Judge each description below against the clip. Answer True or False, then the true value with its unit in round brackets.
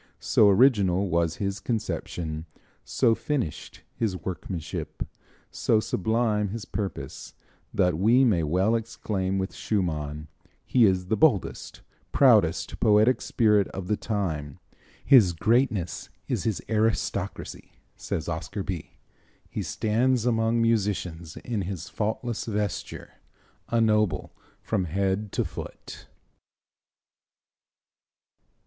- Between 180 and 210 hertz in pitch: False (100 Hz)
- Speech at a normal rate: False (110 wpm)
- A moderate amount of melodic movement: True (3.9 semitones)